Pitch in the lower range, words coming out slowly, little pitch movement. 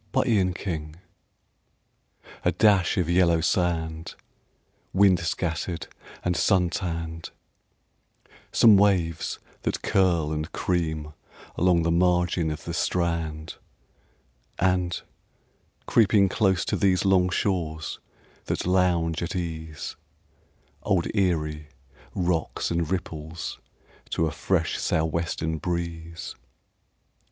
Yes: very low, 85 Hz; slow, 100 wpm; narrow, 2.2 semitones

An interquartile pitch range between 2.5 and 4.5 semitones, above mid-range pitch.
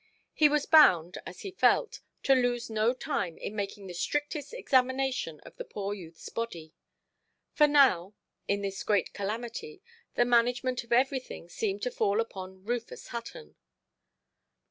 No: average, 5.2 semitones; high, 235 Hz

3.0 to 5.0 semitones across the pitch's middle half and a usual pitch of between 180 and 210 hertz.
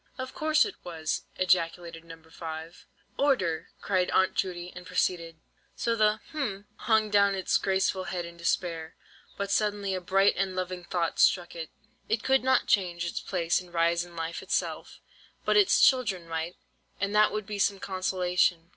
Yes: average, 3.3 semitones; medium, 185 Hz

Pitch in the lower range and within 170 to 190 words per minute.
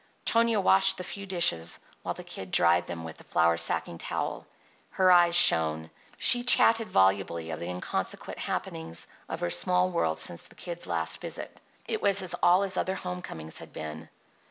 Yes: very low, 90 Hz; average, 180 wpm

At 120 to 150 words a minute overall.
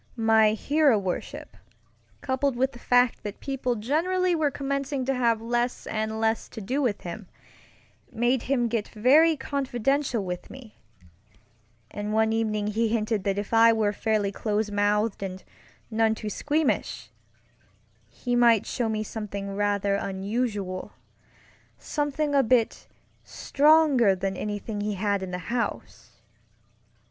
Yes: slow, 135 wpm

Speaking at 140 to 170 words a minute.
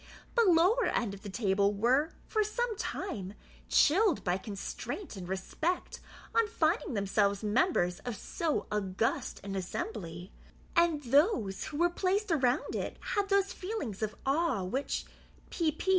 Yes: average, 145 wpm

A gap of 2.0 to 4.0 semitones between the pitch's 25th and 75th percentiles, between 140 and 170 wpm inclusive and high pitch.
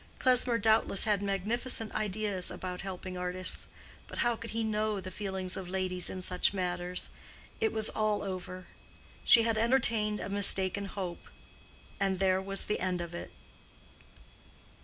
Yes: average, 2.8 semitones; average, 150 wpm; high, 195 Hz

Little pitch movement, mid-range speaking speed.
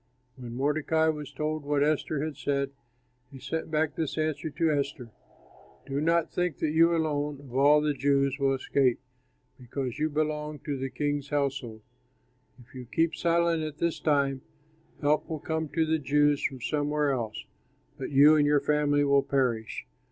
Yes: narrow, 2.2 semitones; average, 170 wpm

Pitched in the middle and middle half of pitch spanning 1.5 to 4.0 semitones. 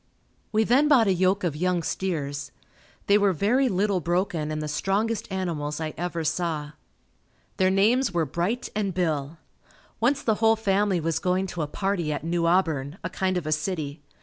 No: medium, 180 Hz; average, 4.4 semitones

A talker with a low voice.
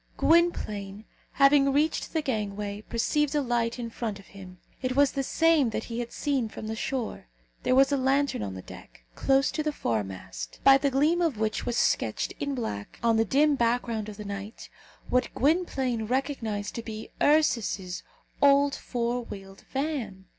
No: high, 240 Hz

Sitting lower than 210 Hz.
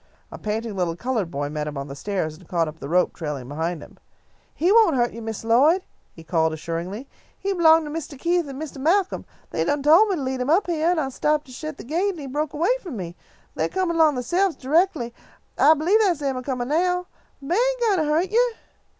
No: very high, 285 Hz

